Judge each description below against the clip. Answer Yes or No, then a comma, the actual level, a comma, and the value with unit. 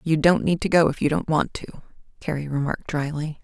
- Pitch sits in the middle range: Yes, medium, 160 Hz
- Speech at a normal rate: No, fast, 225 wpm